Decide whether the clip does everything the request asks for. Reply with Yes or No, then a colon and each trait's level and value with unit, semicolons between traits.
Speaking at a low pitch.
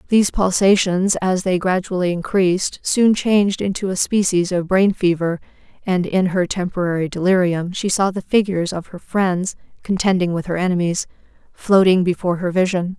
No: medium, 185 Hz